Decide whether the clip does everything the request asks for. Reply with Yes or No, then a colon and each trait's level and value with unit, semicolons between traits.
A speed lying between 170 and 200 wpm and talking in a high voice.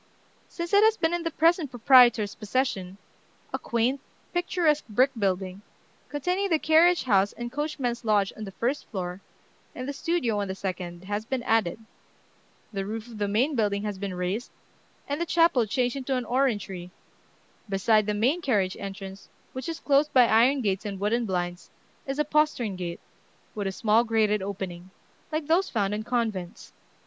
Yes: average, 175 wpm; high, 225 Hz